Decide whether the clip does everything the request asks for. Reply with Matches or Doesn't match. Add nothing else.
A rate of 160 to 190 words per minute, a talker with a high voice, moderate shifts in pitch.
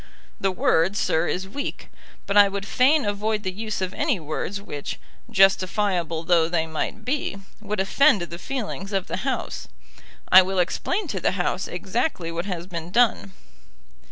Matches